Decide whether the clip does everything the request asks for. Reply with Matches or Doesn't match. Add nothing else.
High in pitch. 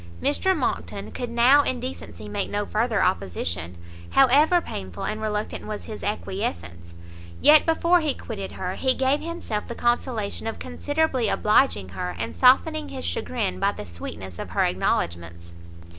Matches